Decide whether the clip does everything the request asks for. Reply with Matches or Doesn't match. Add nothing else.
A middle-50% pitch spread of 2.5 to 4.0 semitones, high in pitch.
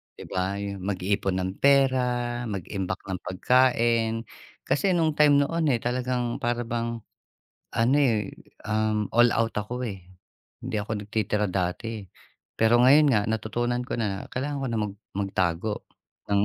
Doesn't match